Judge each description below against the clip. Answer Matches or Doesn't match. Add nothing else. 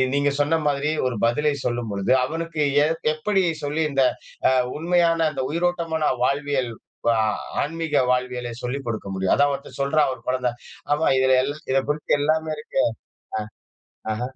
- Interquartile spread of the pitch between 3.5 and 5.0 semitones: Matches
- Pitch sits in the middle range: Matches